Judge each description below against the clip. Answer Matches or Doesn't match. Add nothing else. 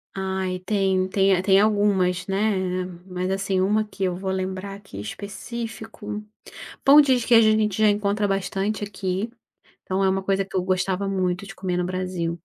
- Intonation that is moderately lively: Doesn't match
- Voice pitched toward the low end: Doesn't match